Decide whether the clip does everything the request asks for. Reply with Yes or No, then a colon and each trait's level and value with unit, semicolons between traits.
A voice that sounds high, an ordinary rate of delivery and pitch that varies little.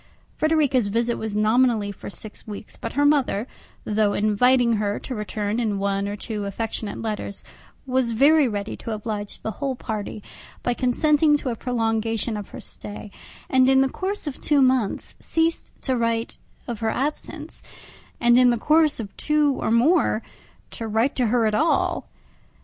No: high, 230 Hz; average, 165 wpm; average, 3.8 semitones